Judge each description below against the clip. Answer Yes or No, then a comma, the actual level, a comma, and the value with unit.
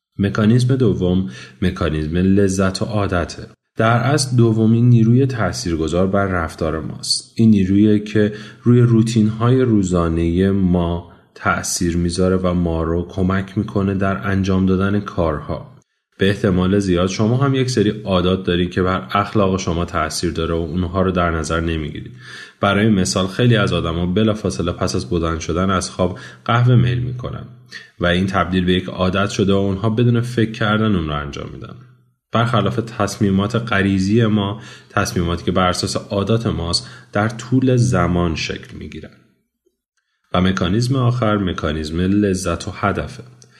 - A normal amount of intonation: Yes, average, 3.9 semitones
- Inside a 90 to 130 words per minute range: No, average, 145 wpm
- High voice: No, low, 100 Hz